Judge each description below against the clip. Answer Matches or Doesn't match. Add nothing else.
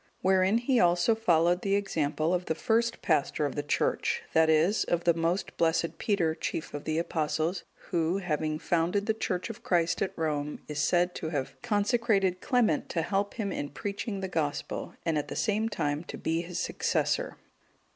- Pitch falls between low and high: Matches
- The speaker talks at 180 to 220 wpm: Matches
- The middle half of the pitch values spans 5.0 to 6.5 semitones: Doesn't match